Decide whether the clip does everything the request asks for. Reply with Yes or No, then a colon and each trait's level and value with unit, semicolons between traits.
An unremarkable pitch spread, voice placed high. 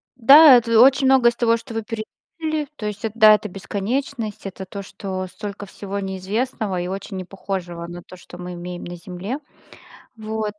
Yes: average, 3.7 semitones; high, 210 Hz